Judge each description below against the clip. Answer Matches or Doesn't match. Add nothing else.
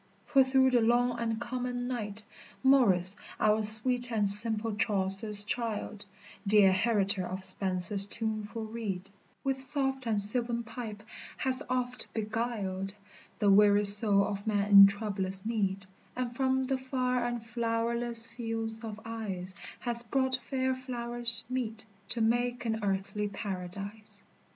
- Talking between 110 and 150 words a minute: Matches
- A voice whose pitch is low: Doesn't match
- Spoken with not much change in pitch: Doesn't match